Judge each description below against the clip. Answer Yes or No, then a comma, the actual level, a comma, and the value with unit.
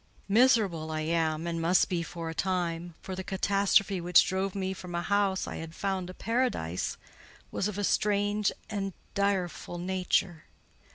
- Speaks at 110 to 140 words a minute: No, average, 165 wpm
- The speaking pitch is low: No, medium, 185 Hz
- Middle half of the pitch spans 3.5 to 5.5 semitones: No, average, 2.8 semitones